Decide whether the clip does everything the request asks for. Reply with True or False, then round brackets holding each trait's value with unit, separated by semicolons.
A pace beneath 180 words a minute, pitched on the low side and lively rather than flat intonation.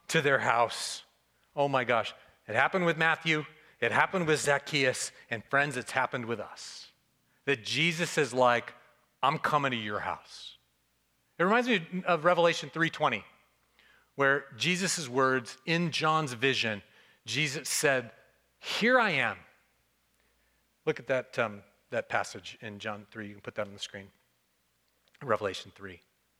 True (145 wpm; 130 Hz; 6.5 semitones)